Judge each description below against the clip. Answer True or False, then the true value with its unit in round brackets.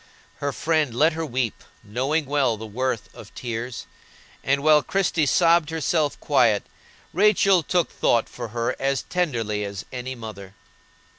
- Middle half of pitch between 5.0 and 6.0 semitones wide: True (5.4 semitones)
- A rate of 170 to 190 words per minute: False (145 wpm)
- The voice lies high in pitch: False (135 Hz)